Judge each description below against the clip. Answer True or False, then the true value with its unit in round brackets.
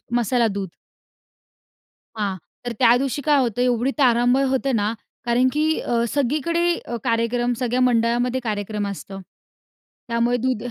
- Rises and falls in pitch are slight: True (2.0 semitones)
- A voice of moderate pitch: False (240 Hz)